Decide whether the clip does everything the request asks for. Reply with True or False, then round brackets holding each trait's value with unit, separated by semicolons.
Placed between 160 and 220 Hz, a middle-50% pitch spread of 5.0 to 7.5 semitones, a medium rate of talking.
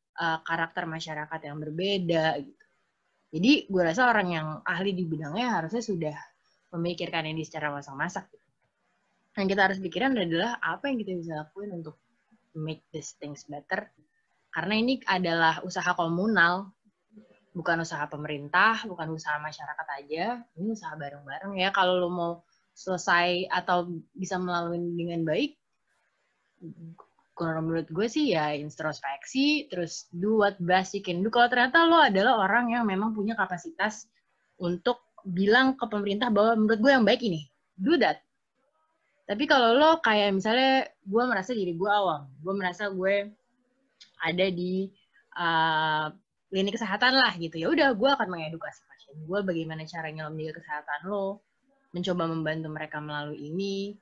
False (185 Hz; 5.3 semitones; 145 wpm)